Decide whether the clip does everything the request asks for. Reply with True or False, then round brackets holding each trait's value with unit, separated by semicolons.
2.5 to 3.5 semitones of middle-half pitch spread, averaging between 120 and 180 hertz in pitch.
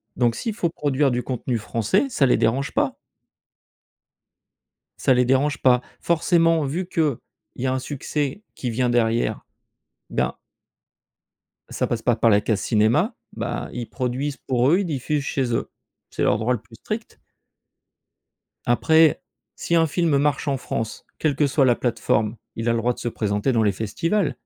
False (4.3 semitones; 130 Hz)